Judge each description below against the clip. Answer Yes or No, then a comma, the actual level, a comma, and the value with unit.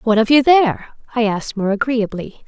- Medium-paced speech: Yes, average, 195 wpm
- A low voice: No, high, 230 Hz